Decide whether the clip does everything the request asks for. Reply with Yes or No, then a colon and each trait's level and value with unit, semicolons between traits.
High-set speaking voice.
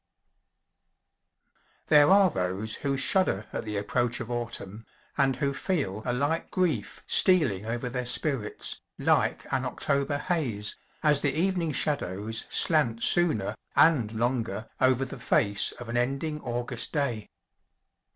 No: low, 125 Hz